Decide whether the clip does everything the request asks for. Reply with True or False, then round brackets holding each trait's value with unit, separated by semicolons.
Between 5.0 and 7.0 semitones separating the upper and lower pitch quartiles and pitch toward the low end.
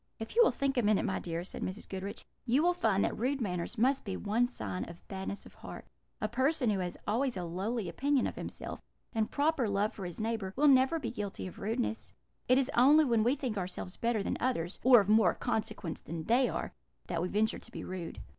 False (5.3 semitones; 220 Hz)